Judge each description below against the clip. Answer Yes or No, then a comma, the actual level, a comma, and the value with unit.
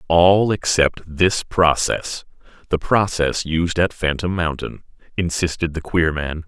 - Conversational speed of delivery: No, slow, 120 wpm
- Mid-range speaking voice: No, very low, 85 Hz